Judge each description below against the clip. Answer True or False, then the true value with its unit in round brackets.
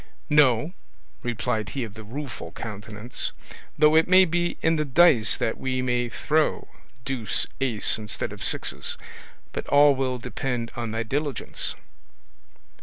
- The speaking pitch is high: False (125 Hz)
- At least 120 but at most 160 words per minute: True (140 wpm)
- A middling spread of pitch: True (4.6 semitones)